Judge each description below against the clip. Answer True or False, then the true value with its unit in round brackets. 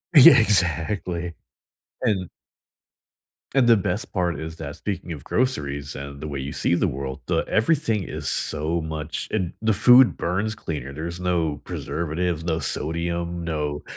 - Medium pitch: False (85 Hz)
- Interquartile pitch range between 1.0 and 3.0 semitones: False (4.6 semitones)